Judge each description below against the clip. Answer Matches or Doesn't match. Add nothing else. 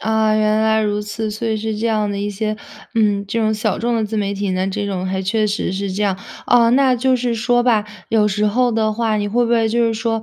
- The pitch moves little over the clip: Matches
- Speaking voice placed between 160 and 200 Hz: Doesn't match